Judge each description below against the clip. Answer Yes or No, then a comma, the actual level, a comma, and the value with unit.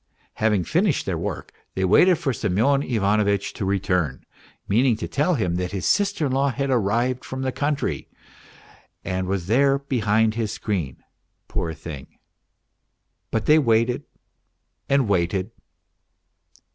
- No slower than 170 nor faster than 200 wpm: No, slow, 135 wpm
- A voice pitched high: No, low, 110 Hz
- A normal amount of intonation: No, wide, 6.0 semitones